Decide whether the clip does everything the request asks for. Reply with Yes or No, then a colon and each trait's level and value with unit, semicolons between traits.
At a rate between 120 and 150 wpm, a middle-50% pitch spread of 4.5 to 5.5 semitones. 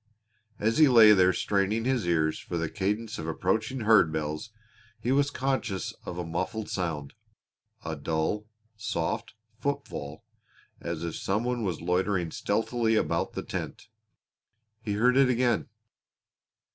Yes: average, 140 wpm; average, 5.2 semitones